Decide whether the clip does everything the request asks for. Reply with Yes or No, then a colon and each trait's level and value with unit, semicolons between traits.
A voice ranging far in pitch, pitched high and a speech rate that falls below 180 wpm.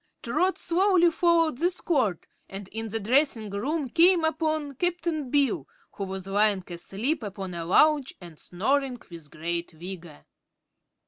Yes: wide, 8.8 semitones; high, 245 Hz; average, 140 wpm